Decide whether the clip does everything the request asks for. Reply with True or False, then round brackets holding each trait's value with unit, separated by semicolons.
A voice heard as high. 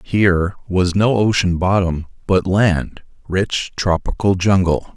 False (95 Hz)